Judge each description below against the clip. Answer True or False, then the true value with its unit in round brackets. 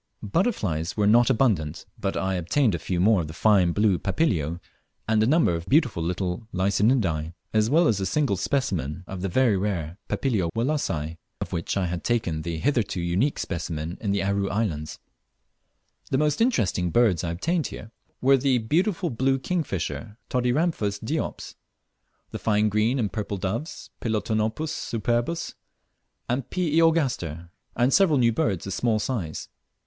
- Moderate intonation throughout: False (6.7 semitones)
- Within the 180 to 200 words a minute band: False (160 wpm)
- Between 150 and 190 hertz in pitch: False (105 Hz)